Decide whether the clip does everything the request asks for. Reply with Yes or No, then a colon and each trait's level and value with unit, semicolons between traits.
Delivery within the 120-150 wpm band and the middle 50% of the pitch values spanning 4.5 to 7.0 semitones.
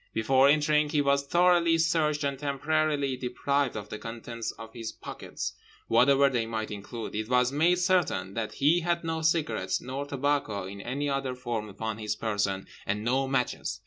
No: average, 175 wpm; average, 4.9 semitones